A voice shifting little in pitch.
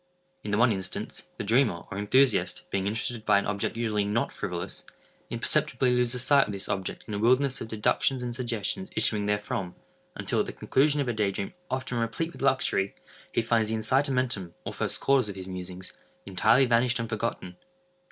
No: average, 4.1 semitones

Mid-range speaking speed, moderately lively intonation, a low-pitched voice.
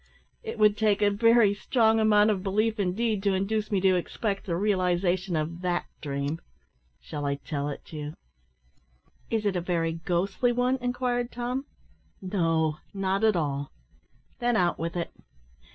No: average, 155 wpm; average, 4.5 semitones; high, 195 Hz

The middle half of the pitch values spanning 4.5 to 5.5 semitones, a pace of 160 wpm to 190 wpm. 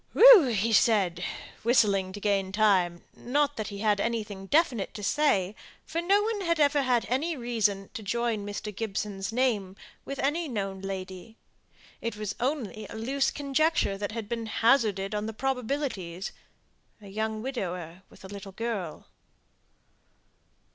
No: average, 5.1 semitones; average, 150 wpm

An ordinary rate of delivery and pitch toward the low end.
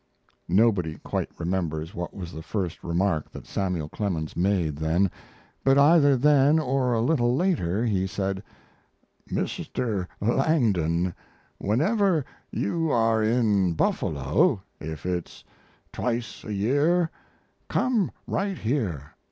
No: slow, 115 wpm; low, 105 Hz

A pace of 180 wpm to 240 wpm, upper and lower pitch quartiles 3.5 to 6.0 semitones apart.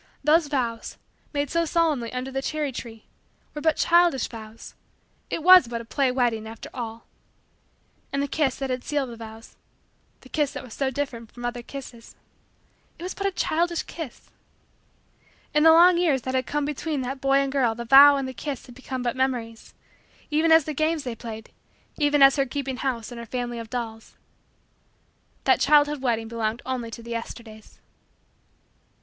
Yes: average, 185 wpm; average, 4.0 semitones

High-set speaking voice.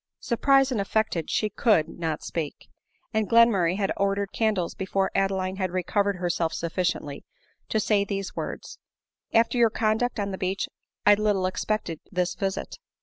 Yes: high, 195 Hz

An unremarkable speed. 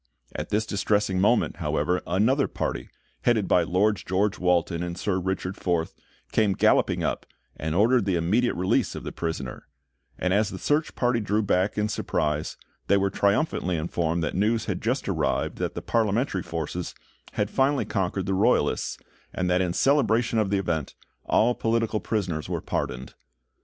Yes: average, 170 wpm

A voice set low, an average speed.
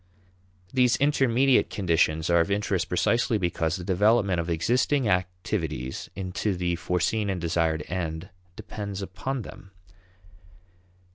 No: very low, 95 Hz; slow, 120 wpm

